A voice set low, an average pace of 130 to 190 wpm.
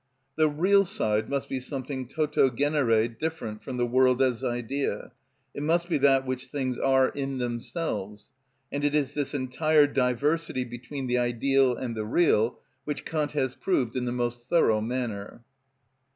Yes: low, 130 Hz; average, 165 wpm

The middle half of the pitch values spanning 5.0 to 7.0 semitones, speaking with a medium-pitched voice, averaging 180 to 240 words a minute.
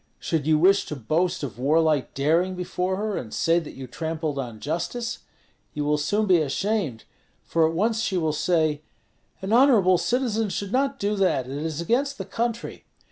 Yes: wide, 5.6 semitones; medium, 175 Hz; average, 185 wpm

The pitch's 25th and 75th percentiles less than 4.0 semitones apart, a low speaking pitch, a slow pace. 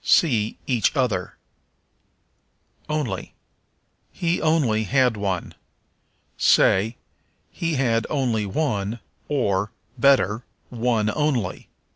No: average, 4.8 semitones; low, 120 Hz; slow, 85 wpm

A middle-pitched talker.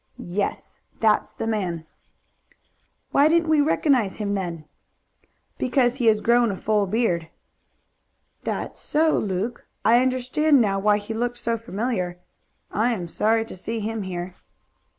No: high, 220 Hz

